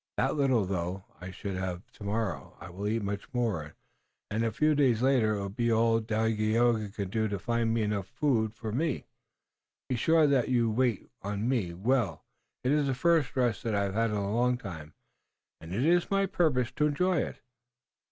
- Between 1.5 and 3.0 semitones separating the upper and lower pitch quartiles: No, average, 4.1 semitones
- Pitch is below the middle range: Yes, low, 115 Hz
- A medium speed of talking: Yes, average, 195 wpm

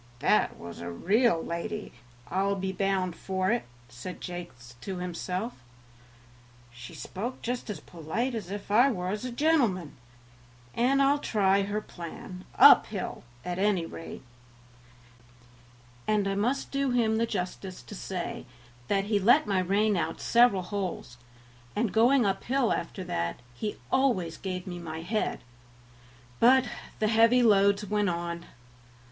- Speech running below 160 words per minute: Yes, average, 140 wpm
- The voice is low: No, high, 195 Hz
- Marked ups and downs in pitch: No, average, 4.2 semitones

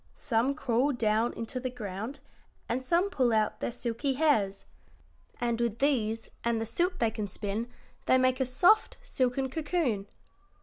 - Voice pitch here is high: Yes, high, 245 Hz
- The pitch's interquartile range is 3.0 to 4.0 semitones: Yes, average, 3.7 semitones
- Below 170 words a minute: Yes, average, 160 wpm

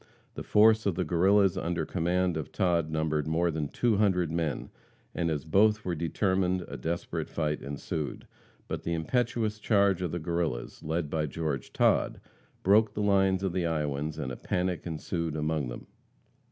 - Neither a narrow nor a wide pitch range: Yes, average, 3.6 semitones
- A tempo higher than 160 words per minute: Yes, average, 170 wpm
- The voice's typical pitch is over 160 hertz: No, very low, 85 Hz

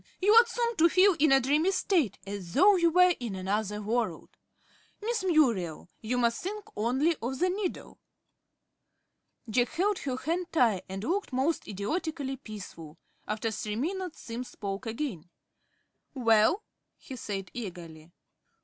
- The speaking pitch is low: No, very high, 255 Hz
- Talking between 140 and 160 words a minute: Yes, average, 145 wpm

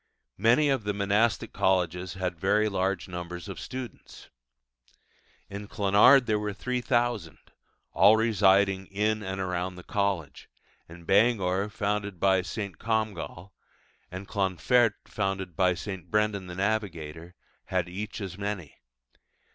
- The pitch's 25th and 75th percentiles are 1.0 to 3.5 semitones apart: Yes, average, 2.7 semitones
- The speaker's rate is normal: No, slow, 125 wpm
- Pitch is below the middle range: Yes, low, 100 Hz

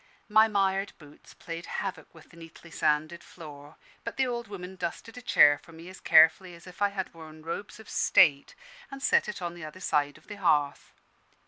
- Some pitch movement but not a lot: Yes, average, 4.2 semitones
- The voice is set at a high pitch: No, medium, 170 Hz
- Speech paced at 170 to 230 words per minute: Yes, fast, 205 wpm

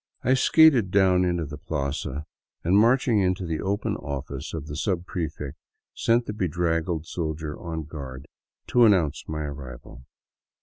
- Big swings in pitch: No, average, 4.6 semitones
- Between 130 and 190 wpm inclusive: Yes, average, 140 wpm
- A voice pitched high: No, very low, 80 Hz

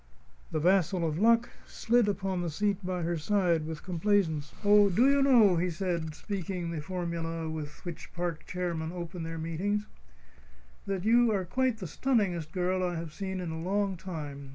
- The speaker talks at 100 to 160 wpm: No, average, 175 wpm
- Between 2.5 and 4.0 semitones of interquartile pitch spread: Yes, average, 3.6 semitones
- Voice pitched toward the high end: No, medium, 180 Hz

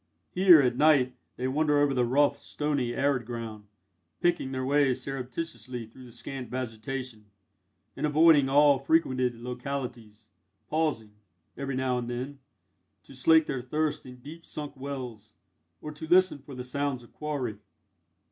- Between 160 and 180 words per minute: No, average, 145 wpm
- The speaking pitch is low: Yes, low, 130 Hz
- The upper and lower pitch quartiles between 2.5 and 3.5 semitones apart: Yes, average, 3.0 semitones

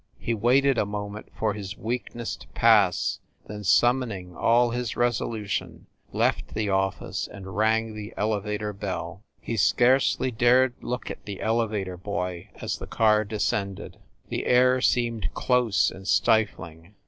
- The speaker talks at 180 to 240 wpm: No, average, 140 wpm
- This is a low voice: Yes, low, 110 Hz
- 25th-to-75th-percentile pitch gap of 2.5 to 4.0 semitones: Yes, average, 3.1 semitones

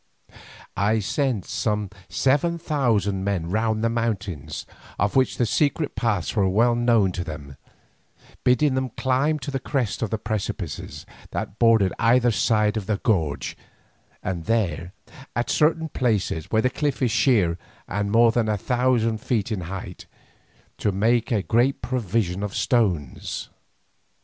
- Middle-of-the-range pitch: No, low, 110 Hz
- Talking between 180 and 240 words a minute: No, average, 150 wpm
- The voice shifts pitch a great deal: No, average, 4.0 semitones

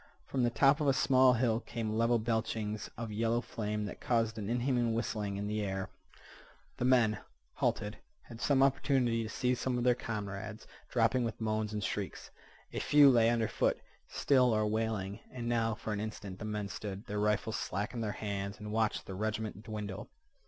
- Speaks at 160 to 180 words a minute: No, average, 190 wpm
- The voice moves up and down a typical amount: No, narrow, 2.2 semitones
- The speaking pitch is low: Yes, low, 110 Hz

